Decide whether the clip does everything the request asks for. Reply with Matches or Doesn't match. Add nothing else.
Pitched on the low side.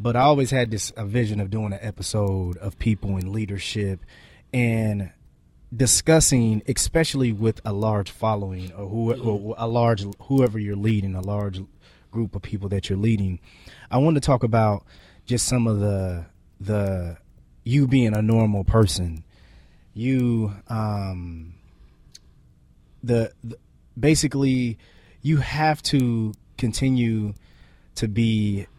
Matches